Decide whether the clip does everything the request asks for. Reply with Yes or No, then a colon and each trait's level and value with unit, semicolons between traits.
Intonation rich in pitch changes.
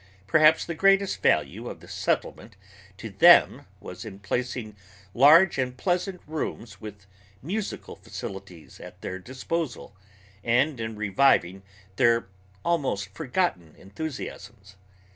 Yes: wide, 8.1 semitones